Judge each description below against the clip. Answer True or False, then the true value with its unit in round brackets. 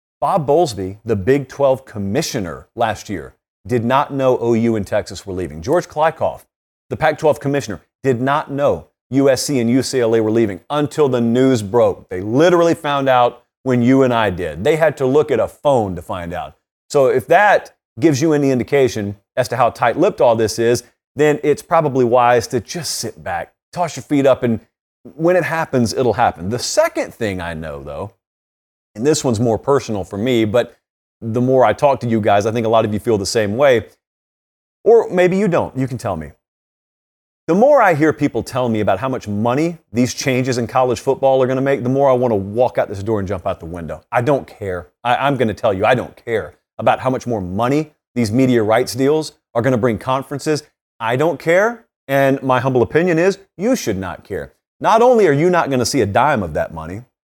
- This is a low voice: True (125 Hz)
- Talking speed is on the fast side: True (215 wpm)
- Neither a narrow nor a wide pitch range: True (4.3 semitones)